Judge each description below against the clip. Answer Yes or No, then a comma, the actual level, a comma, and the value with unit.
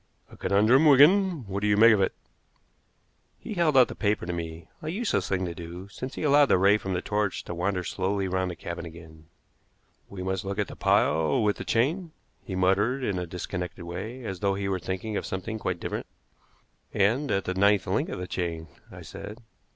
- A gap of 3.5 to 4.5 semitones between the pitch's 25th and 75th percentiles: Yes, average, 3.9 semitones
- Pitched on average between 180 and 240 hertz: No, low, 100 Hz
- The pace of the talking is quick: Yes, fast, 215 wpm